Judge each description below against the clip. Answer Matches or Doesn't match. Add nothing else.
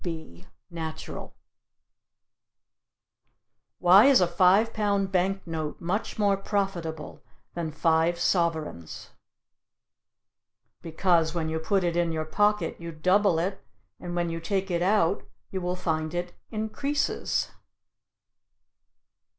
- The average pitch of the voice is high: Doesn't match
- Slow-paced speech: Matches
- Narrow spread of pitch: Doesn't match